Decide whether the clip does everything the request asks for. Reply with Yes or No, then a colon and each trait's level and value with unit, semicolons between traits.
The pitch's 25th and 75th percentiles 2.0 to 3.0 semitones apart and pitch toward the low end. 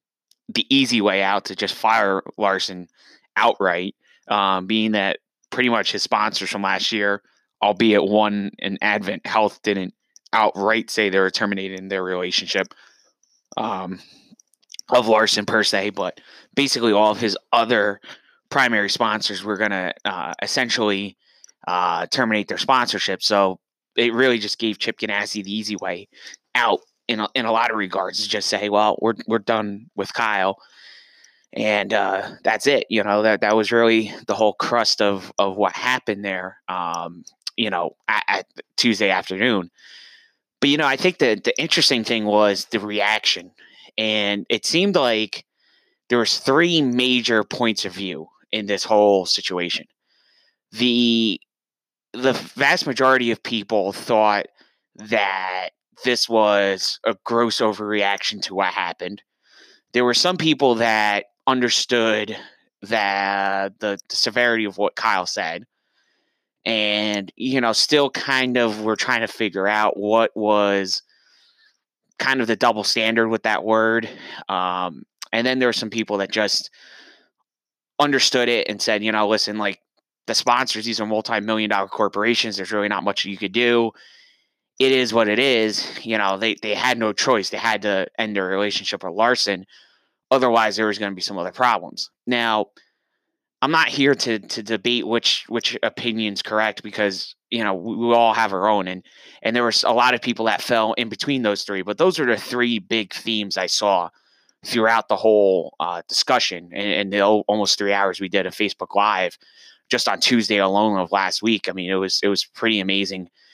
Yes: narrow, 2.4 semitones; low, 110 Hz